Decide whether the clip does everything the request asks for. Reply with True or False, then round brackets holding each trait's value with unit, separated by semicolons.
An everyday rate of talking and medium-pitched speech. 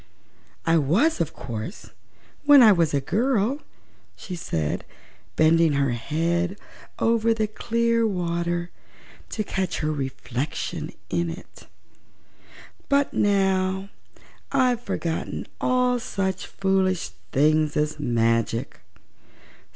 False (105 wpm; 180 Hz)